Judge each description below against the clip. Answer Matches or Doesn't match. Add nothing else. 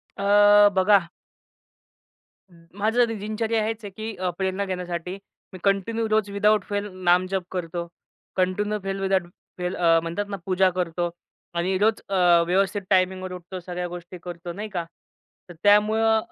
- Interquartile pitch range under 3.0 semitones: Matches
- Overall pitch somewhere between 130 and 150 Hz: Doesn't match